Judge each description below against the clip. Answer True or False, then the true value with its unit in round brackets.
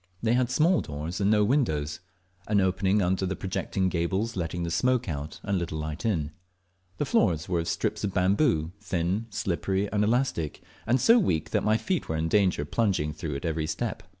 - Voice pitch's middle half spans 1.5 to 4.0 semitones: False (4.8 semitones)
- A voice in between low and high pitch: False (95 Hz)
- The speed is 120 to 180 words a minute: False (205 wpm)